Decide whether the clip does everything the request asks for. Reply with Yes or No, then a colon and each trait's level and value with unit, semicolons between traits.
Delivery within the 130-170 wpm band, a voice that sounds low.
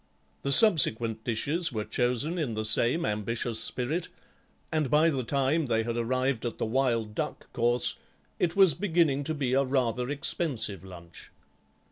Yes: average, 155 wpm; low, 130 Hz